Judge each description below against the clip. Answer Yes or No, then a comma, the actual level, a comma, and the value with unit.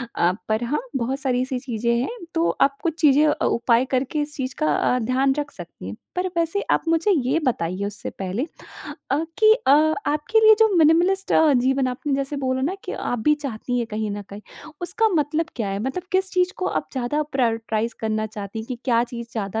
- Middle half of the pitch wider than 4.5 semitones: Yes, average, 5.3 semitones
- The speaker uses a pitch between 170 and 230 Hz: No, very high, 265 Hz